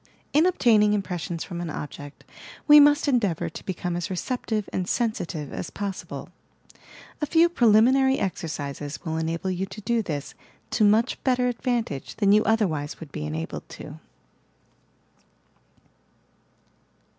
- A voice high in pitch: Yes, high, 200 Hz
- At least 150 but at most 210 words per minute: No, slow, 135 wpm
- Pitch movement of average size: No, wide, 6.6 semitones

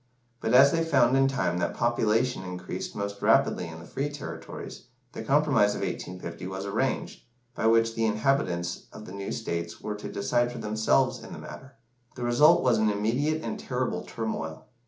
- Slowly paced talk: No, average, 180 wpm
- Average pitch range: Yes, average, 4.6 semitones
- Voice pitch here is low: Yes, low, 110 Hz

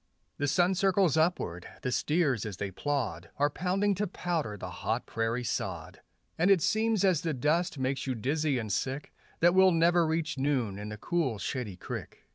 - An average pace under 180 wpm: No, average, 185 wpm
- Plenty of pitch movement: Yes, wide, 6.6 semitones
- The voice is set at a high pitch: No, medium, 150 Hz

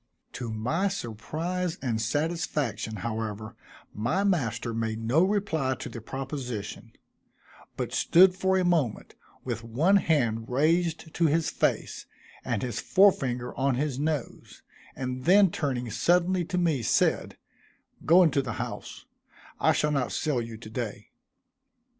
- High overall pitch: No, low, 135 Hz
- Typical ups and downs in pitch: No, wide, 6.5 semitones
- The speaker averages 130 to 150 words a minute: Yes, average, 140 wpm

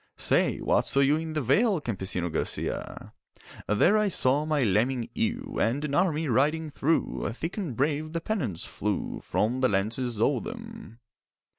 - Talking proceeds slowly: No, average, 160 wpm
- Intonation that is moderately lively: No, wide, 6.0 semitones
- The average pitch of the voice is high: No, medium, 145 Hz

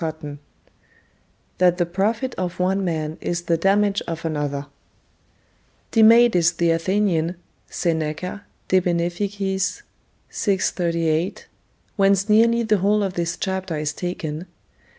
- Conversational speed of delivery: No, slow, 120 wpm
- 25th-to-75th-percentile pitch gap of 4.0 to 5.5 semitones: No, average, 3.2 semitones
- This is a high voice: No, medium, 180 Hz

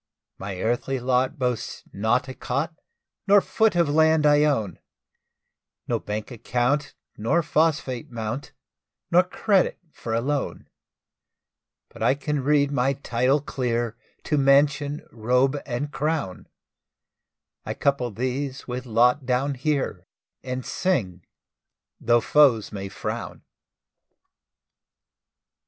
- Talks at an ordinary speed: No, slow, 115 wpm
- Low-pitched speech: Yes, low, 130 Hz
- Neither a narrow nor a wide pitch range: Yes, average, 3.6 semitones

